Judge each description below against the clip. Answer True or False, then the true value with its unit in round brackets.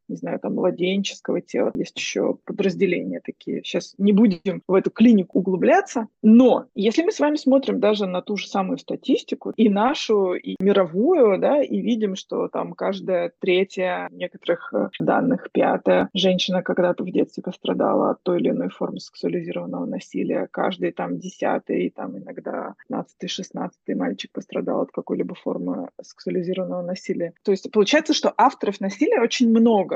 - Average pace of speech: True (150 wpm)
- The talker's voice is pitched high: True (200 Hz)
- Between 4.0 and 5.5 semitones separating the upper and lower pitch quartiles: True (4.5 semitones)